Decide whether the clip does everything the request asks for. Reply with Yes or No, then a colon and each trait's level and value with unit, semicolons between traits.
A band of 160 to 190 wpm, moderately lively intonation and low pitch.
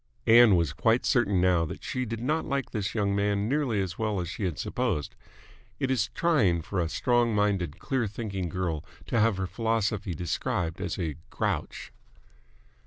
Yes: average, 175 wpm; average, 4.7 semitones; low, 100 Hz